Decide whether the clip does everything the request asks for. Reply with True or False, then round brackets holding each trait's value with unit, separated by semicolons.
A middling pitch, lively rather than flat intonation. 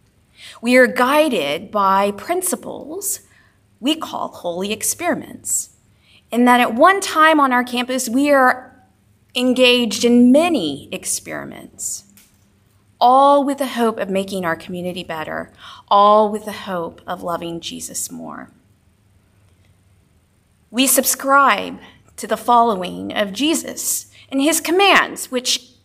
False (240 Hz; 8.2 semitones)